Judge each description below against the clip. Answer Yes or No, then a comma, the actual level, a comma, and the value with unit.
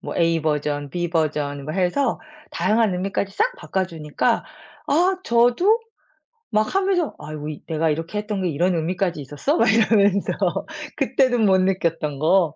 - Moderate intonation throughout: No, wide, 5.9 semitones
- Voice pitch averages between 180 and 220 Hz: Yes, medium, 185 Hz